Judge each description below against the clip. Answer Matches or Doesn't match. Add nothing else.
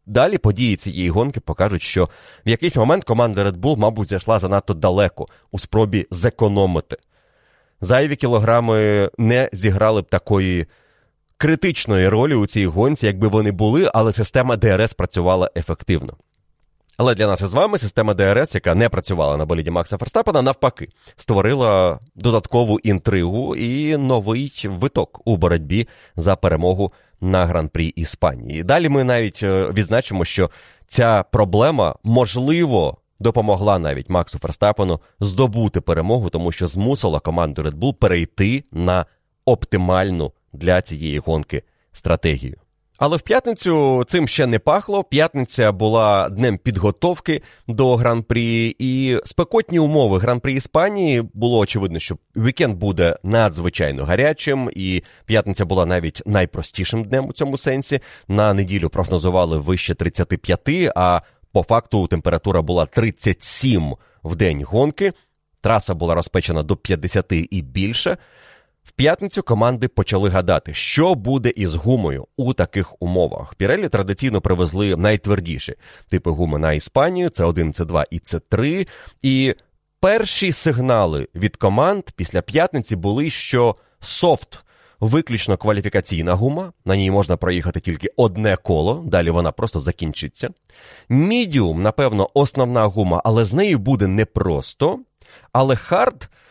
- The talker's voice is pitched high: Doesn't match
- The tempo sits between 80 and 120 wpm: Doesn't match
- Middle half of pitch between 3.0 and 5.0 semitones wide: Doesn't match